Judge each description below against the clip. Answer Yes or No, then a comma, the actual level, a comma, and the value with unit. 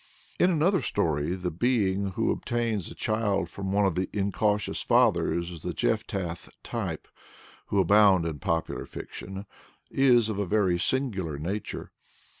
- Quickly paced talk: No, average, 145 wpm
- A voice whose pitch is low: Yes, low, 100 Hz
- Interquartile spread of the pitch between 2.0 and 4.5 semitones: Yes, average, 3.7 semitones